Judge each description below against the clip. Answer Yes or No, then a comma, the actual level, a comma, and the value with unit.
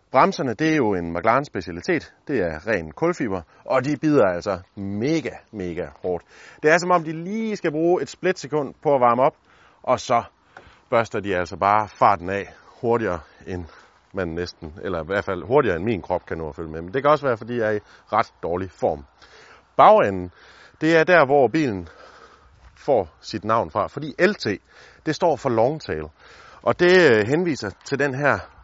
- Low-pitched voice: Yes, low, 120 Hz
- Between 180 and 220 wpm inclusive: Yes, average, 195 wpm